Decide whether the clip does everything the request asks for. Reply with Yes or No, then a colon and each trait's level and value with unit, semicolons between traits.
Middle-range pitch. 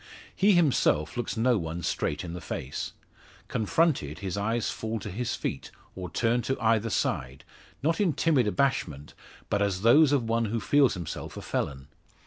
No: low, 110 Hz